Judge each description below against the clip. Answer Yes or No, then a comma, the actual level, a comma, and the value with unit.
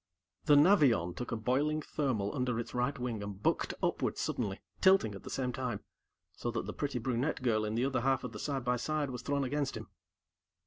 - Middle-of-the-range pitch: No, low, 125 Hz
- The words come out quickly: Yes, fast, 215 wpm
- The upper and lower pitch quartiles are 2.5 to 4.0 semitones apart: Yes, average, 3.4 semitones